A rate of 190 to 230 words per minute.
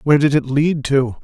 No: fast, 245 wpm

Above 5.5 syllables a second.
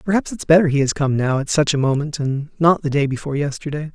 Yes: 6.4 syllables/s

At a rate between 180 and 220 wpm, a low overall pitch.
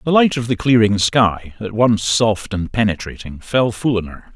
Yes: fast, 205 wpm; low, 110 Hz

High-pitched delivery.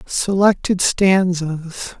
No: medium, 180 Hz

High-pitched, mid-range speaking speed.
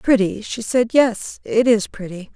Yes: high, 220 Hz; average, 180 wpm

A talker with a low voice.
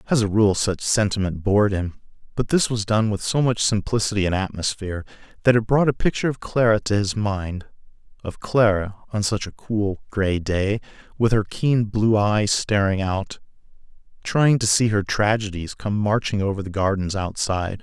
Yes: low, 105 Hz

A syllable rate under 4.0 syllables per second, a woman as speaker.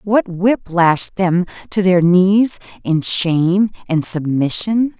Yes: 3.3 syllables/s; female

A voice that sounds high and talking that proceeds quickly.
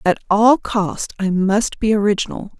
No: high, 205 Hz; average, 160 wpm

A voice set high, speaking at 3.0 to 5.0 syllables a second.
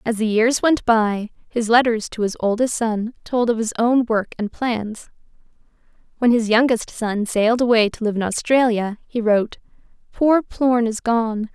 Yes: high, 230 Hz; 4.5 syllables/s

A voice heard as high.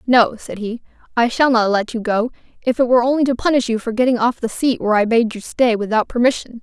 Yes: high, 235 Hz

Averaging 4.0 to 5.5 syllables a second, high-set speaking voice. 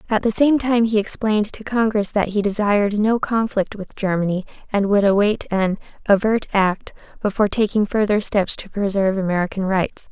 Yes: 5.3 syllables/s; high, 205 Hz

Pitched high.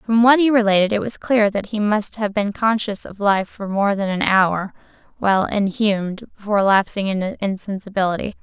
Yes: high, 205 Hz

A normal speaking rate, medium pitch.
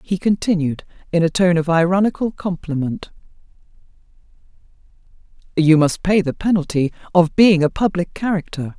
No: slow, 125 wpm; medium, 175 Hz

